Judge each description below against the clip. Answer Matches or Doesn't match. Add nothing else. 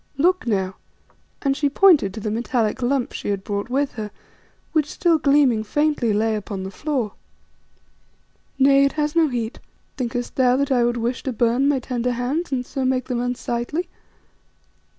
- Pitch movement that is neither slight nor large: Matches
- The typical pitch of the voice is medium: Doesn't match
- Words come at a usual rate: Matches